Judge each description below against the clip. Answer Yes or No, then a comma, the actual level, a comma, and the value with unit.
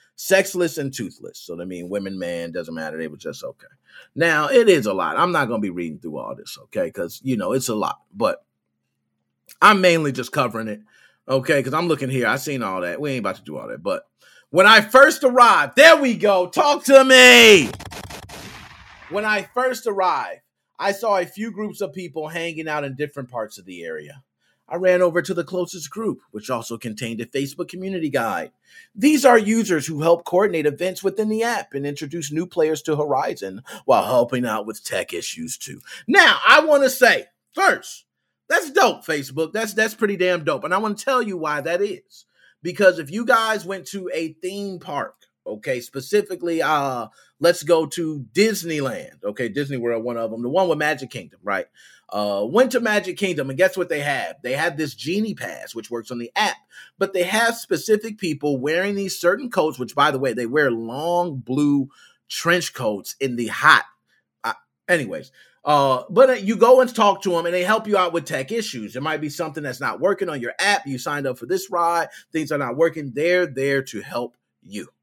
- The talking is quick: Yes, fast, 210 wpm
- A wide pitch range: Yes, wide, 7.3 semitones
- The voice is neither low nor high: Yes, medium, 170 Hz